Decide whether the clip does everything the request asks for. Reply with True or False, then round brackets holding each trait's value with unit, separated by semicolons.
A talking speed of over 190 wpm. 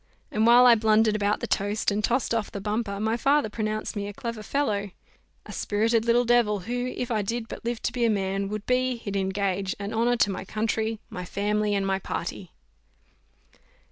True (205 wpm)